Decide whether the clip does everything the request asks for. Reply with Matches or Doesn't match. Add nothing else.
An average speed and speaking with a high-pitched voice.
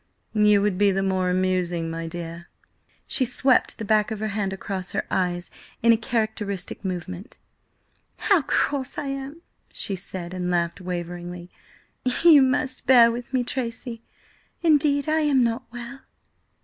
Matches